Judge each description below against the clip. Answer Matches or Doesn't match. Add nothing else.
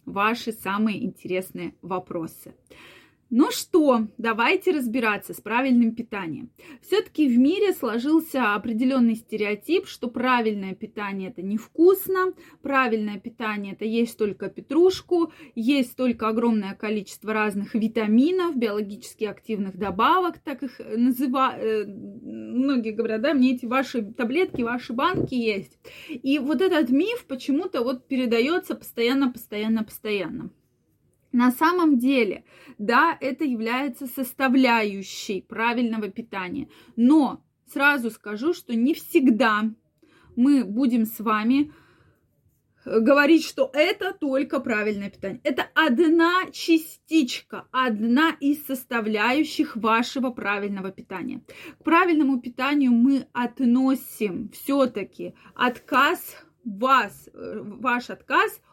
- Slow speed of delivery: Matches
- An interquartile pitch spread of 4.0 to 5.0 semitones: Matches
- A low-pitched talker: Doesn't match